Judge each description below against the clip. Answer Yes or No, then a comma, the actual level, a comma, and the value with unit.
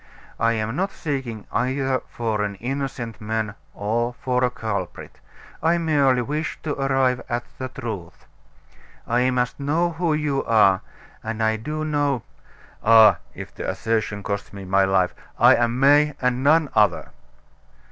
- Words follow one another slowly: No, average, 150 wpm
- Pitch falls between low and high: No, low, 125 Hz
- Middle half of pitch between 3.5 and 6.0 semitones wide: Yes, average, 4.2 semitones